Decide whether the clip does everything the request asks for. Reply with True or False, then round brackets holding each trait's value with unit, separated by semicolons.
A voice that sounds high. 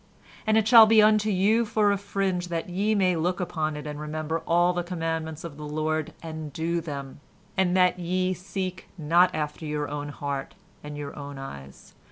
False (170 Hz)